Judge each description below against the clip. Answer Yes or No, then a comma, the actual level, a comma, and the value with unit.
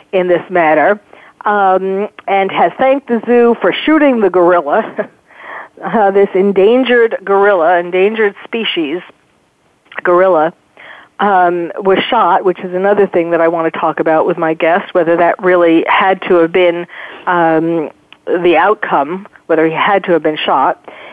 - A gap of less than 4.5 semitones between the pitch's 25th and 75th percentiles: Yes, average, 2.9 semitones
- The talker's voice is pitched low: No, medium, 185 Hz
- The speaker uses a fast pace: No, average, 150 wpm